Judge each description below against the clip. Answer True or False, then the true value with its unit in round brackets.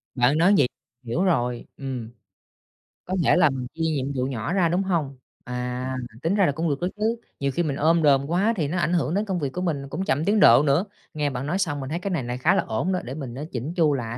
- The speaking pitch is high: False (145 Hz)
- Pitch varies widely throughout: False (5.0 semitones)